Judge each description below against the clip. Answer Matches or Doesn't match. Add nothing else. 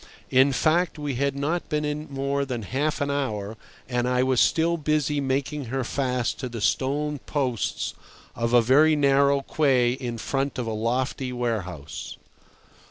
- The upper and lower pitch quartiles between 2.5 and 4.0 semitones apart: Matches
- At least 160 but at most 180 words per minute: Matches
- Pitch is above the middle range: Doesn't match